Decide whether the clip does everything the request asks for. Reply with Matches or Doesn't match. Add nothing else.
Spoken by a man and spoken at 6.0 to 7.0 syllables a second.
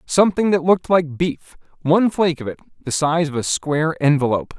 Matches